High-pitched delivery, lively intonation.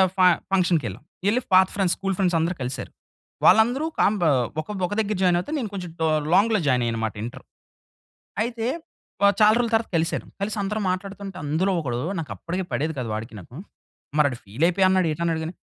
No: medium, 180 Hz; wide, 5.8 semitones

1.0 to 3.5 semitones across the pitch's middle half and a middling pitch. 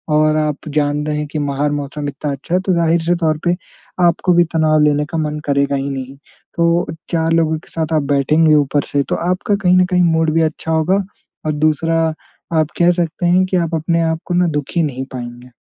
Yes: narrow, 2.6 semitones; medium, 155 Hz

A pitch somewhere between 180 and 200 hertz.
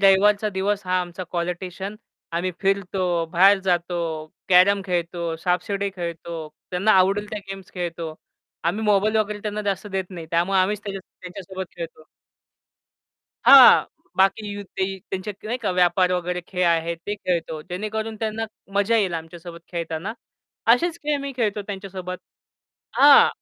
Yes: high, 190 Hz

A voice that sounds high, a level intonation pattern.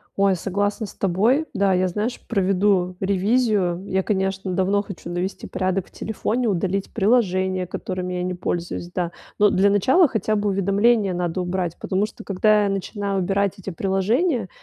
Yes: high, 195 Hz; narrow, 2.0 semitones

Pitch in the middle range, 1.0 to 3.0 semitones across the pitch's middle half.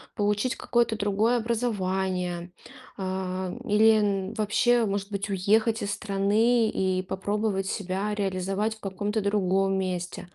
No: high, 200 Hz; narrow, 2.4 semitones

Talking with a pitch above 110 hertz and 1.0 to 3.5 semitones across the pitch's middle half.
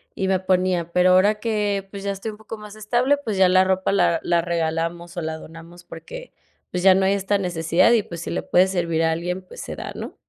Yes: medium, 185 Hz; average, 2.8 semitones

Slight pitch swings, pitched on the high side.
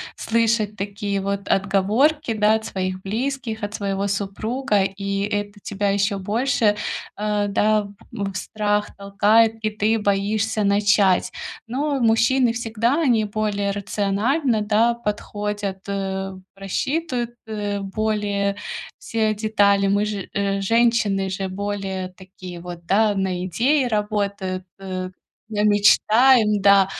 Yes: narrow, 2.0 semitones; high, 205 Hz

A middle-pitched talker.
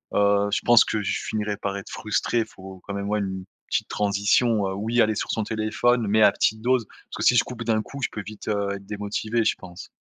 No: low, 105 Hz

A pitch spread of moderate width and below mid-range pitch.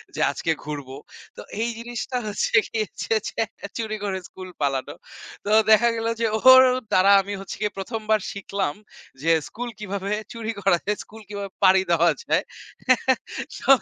No: average, 3.1 semitones; high, 200 Hz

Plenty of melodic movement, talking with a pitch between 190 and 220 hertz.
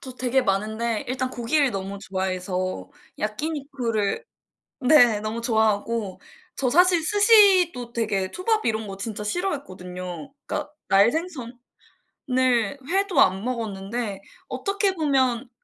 No: wide, 6.4 semitones; high, 235 Hz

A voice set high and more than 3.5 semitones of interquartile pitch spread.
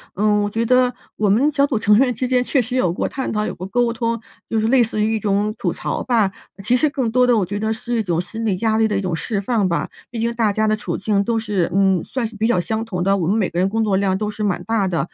No: high, 215 Hz; average, 2.9 semitones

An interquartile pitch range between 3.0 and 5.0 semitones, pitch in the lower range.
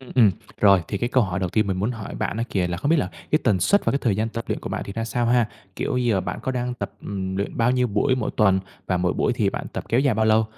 Yes: average, 4.0 semitones; low, 110 Hz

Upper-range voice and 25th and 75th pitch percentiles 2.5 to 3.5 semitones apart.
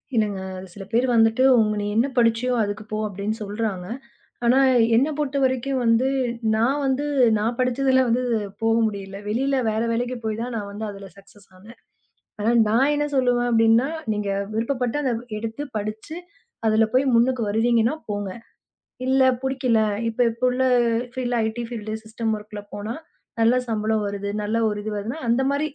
Yes: high, 230 Hz; average, 3.0 semitones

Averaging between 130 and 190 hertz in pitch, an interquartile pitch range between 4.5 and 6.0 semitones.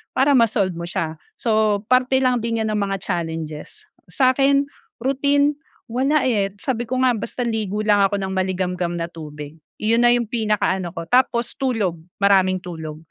No: high, 215 Hz; average, 5.2 semitones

